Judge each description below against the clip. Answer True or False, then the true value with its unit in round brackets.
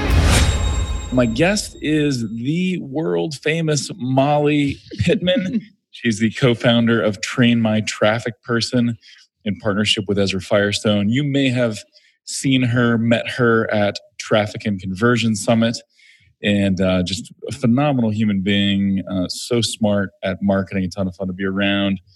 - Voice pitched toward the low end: True (115 Hz)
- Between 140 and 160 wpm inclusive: True (145 wpm)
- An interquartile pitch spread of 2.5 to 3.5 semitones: False (4.0 semitones)